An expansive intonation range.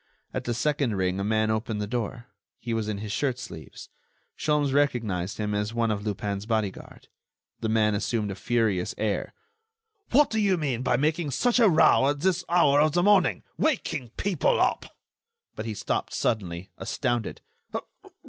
Yes: wide, 5.9 semitones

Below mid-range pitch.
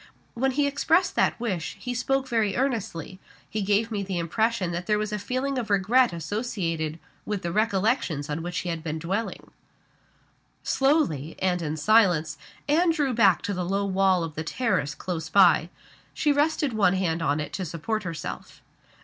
No: high, 200 Hz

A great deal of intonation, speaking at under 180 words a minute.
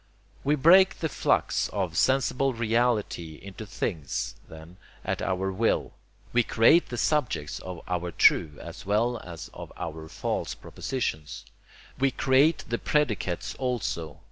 Yes: wide, 7.5 semitones; slow, 135 wpm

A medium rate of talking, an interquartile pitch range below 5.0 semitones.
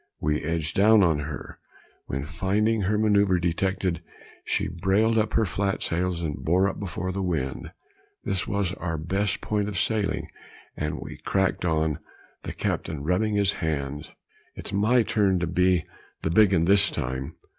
Yes: average, 165 wpm; average, 3.8 semitones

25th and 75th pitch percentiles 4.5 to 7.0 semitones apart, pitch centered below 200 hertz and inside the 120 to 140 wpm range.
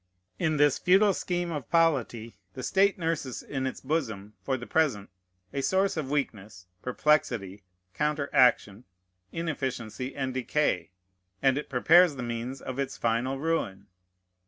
Yes: average, 5.0 semitones; low, 135 Hz; slow, 135 wpm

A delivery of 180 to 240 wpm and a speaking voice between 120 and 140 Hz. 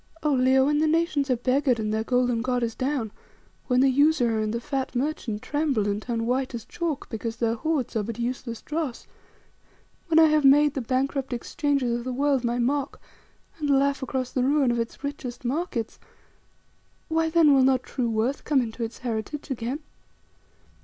No: average, 185 wpm; very high, 260 Hz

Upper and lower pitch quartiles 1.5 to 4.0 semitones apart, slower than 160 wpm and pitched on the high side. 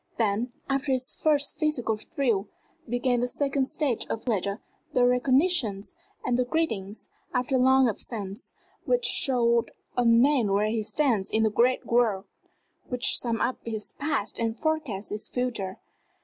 Yes: average, 3.6 semitones; average, 150 wpm; high, 245 Hz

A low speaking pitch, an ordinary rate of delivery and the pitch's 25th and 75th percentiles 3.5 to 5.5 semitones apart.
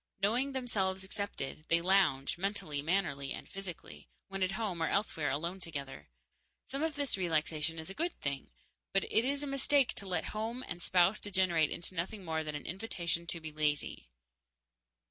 No: medium, 185 Hz; average, 175 wpm; average, 4.7 semitones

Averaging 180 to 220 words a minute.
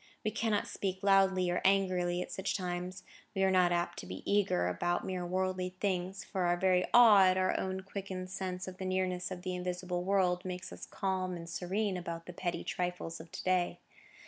Yes: average, 200 wpm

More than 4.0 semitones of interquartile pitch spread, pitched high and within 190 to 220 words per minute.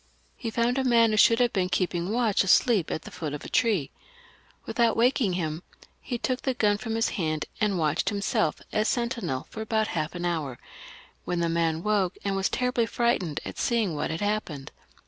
Yes: wide, 5.6 semitones; high, 205 Hz; average, 200 wpm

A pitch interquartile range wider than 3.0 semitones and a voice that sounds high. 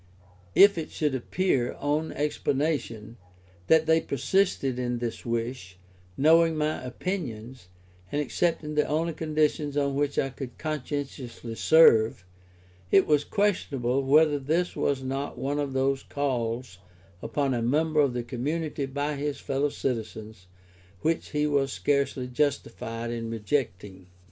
No: average, 3.8 semitones; medium, 140 Hz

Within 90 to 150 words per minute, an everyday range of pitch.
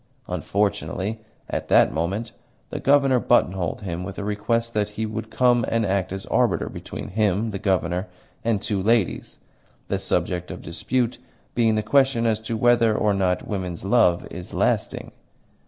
No: average, 160 wpm; average, 3.4 semitones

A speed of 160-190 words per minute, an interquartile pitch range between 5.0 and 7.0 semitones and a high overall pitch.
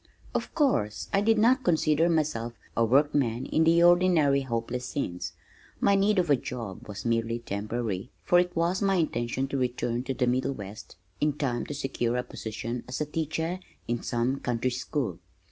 No: average, 175 wpm; wide, 5.6 semitones; low, 130 Hz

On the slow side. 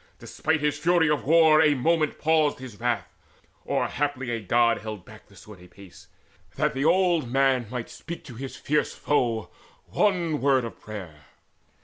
No: average, 170 wpm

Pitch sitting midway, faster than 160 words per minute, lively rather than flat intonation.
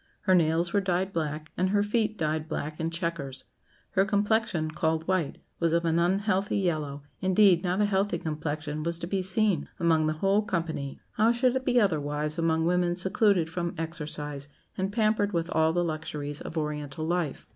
No: medium, 170 Hz; average, 180 wpm; average, 3.6 semitones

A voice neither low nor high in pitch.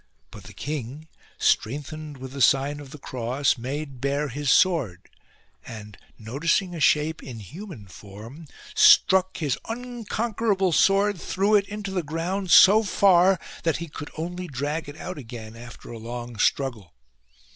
Yes: medium, 150 Hz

